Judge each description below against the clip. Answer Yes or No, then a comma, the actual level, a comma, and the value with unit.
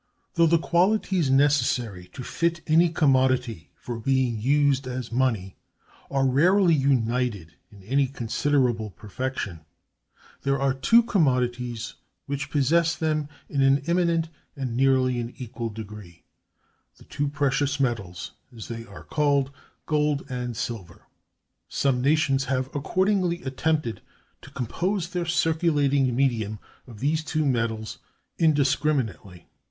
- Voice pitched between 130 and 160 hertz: Yes, low, 135 Hz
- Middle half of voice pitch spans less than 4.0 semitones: No, average, 4.3 semitones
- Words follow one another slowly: Yes, slow, 120 wpm